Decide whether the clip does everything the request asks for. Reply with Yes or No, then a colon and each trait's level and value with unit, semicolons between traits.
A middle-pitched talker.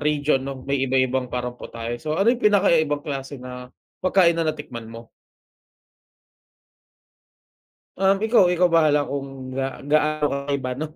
Yes: medium, 145 Hz